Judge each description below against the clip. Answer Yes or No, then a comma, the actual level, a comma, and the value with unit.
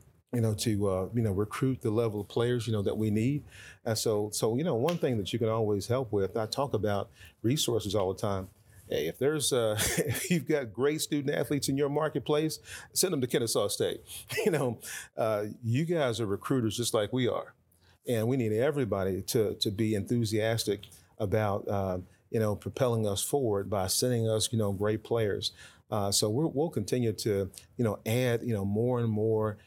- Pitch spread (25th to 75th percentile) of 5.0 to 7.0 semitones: No, average, 3.2 semitones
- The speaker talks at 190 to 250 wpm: Yes, average, 200 wpm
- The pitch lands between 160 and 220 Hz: No, low, 110 Hz